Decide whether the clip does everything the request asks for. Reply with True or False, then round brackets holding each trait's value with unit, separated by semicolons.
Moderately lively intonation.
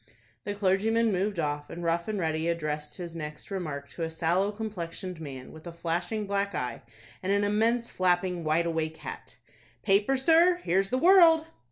True (4.3 semitones)